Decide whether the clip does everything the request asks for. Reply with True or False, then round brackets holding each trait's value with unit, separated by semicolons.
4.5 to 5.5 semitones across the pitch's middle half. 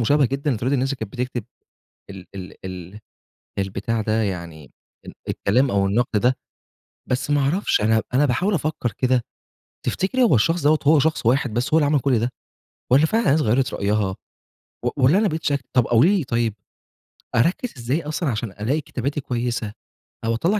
True (5.0 semitones)